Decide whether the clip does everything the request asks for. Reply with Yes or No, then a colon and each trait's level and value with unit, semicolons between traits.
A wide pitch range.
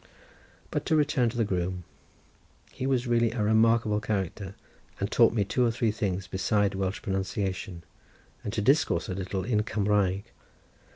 No: average, 3.3 semitones